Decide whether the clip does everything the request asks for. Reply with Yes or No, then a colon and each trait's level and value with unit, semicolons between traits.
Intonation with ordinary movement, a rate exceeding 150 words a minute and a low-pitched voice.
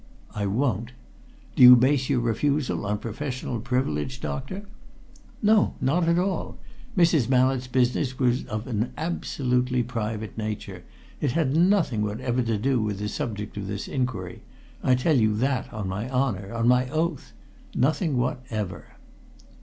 No: average, 4.0 semitones; average, 145 wpm; low, 125 Hz